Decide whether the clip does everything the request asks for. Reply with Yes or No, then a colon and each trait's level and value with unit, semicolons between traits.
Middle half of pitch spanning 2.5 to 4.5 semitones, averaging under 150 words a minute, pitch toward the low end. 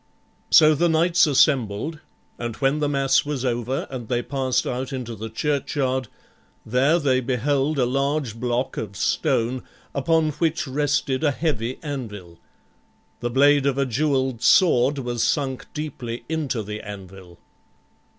Yes: average, 3.4 semitones; average, 140 wpm; low, 130 Hz